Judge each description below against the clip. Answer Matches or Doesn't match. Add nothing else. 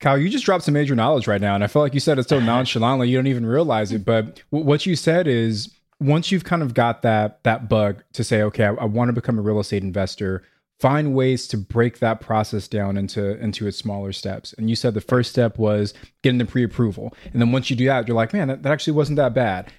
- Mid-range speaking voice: Doesn't match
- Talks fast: Matches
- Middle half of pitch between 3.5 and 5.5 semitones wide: Matches